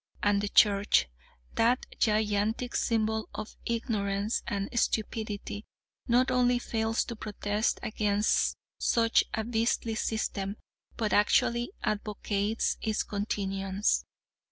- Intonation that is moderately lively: No, narrow, 1.9 semitones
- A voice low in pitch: No, high, 215 Hz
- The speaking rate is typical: No, slow, 105 wpm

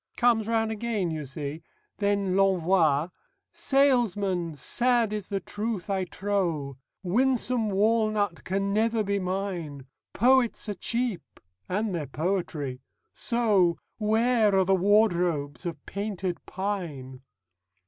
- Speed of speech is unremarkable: No, slow, 115 wpm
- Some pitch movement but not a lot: Yes, average, 4.2 semitones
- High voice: Yes, high, 195 Hz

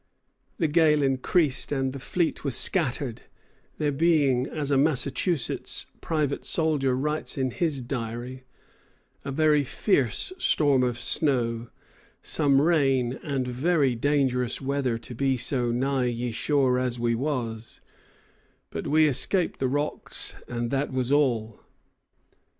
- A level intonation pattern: No, average, 3.1 semitones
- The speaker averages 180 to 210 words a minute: No, slow, 135 wpm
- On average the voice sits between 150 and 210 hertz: No, low, 135 Hz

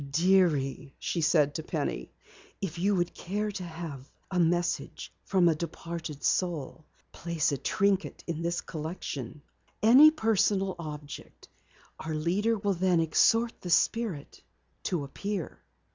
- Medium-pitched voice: Yes, medium, 170 Hz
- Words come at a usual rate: No, slow, 130 wpm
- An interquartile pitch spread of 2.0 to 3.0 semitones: No, average, 3.8 semitones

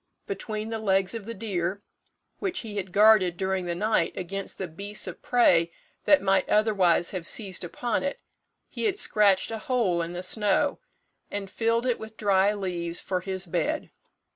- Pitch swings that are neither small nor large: Yes, average, 3.1 semitones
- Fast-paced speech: No, average, 175 wpm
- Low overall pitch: No, high, 200 Hz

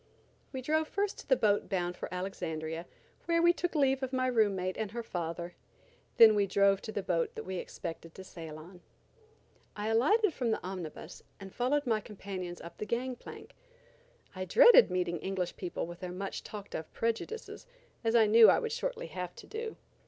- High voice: Yes, high, 205 Hz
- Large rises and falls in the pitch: Yes, wide, 6.2 semitones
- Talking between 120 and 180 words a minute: No, average, 195 wpm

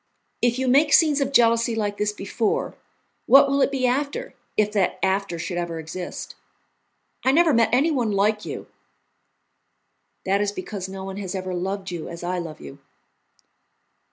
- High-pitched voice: Yes, high, 205 Hz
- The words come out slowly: No, average, 165 wpm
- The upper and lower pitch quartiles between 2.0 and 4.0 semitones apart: No, average, 5.3 semitones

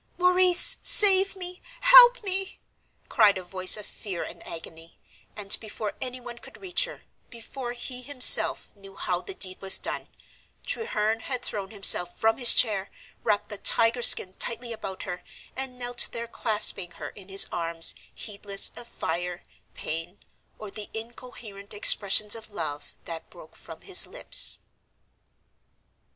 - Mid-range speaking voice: No, high, 215 Hz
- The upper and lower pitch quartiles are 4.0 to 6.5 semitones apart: Yes, average, 4.7 semitones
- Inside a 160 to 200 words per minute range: No, average, 145 wpm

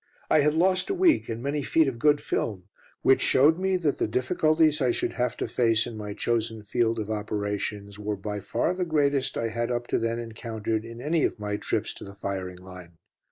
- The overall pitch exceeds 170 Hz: No, low, 115 Hz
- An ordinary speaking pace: No, fast, 215 wpm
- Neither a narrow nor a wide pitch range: No, wide, 5.9 semitones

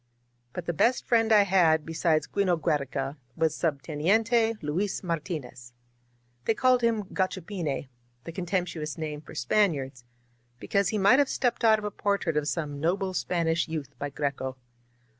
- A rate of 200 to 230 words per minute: No, average, 165 wpm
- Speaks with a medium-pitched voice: Yes, medium, 165 Hz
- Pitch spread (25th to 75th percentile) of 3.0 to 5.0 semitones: No, wide, 5.4 semitones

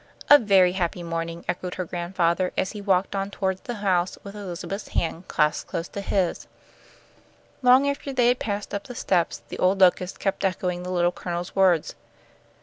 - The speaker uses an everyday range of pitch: No, narrow, 2.3 semitones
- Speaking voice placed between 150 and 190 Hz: Yes, medium, 185 Hz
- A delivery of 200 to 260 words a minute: No, average, 185 wpm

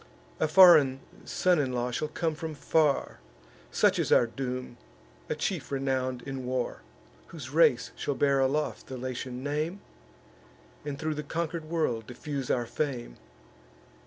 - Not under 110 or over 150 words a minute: Yes, average, 145 wpm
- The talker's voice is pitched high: No, medium, 140 Hz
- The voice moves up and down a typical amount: Yes, average, 3.4 semitones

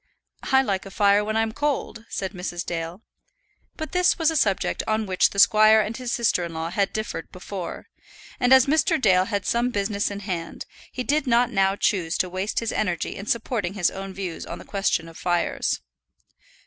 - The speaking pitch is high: Yes, high, 205 Hz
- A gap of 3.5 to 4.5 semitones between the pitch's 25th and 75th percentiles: Yes, average, 4.0 semitones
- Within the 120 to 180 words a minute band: No, average, 200 wpm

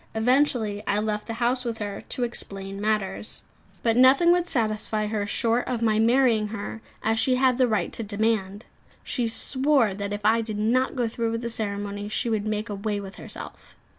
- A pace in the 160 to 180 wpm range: No, average, 195 wpm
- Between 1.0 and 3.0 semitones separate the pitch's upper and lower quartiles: Yes, narrow, 2.6 semitones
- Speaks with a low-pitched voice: No, high, 220 Hz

